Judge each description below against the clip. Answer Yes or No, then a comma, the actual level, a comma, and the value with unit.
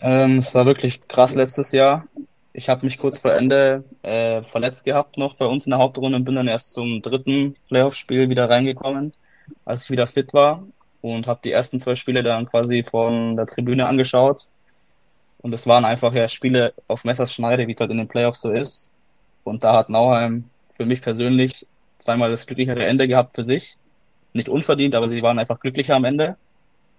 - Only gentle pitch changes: Yes, narrow, 2.2 semitones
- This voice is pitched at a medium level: No, low, 125 Hz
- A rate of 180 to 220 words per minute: Yes, fast, 190 wpm